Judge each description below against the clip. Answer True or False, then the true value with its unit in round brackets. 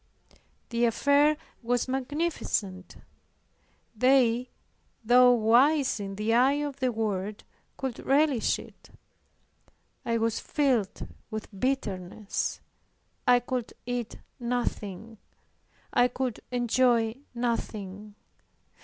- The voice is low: False (240 Hz)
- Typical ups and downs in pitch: True (3.0 semitones)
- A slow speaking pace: True (90 wpm)